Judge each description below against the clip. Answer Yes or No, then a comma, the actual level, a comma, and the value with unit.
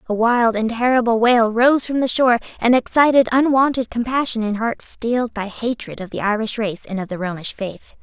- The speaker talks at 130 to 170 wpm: No, average, 200 wpm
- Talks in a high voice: Yes, high, 235 Hz